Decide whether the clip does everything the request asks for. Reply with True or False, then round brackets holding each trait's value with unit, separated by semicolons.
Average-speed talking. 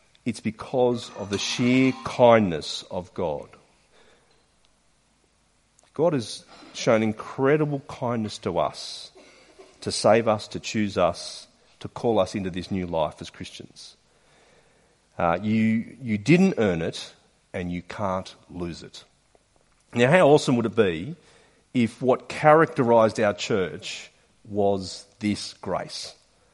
False (125 wpm)